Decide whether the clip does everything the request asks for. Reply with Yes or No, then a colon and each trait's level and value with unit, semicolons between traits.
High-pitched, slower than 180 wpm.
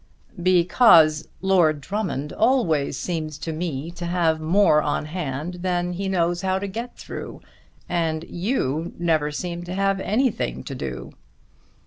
No: medium, 175 Hz; average, 140 wpm